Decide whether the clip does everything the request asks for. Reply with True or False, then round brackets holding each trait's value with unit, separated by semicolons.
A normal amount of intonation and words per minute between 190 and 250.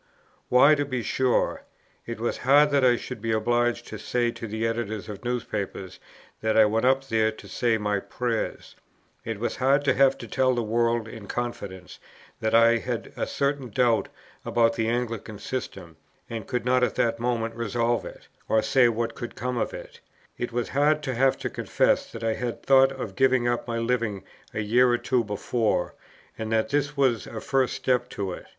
False (2.3 semitones; 195 wpm)